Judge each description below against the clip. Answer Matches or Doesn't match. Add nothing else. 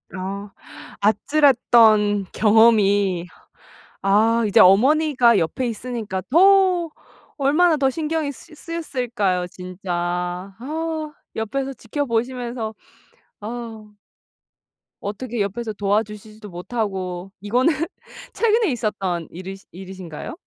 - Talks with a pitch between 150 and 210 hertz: Doesn't match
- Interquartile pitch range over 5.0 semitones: Matches